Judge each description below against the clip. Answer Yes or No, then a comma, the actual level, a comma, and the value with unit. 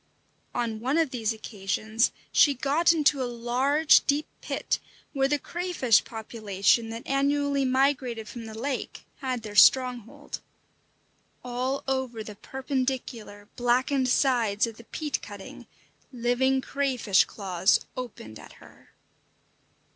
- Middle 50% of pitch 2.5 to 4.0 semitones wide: Yes, average, 3.6 semitones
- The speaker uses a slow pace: Yes, slow, 125 wpm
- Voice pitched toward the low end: No, very high, 250 Hz